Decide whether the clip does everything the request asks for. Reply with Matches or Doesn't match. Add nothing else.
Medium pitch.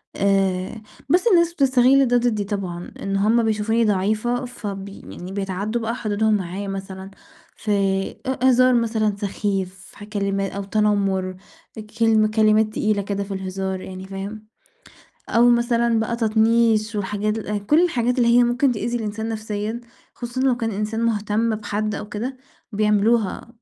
Doesn't match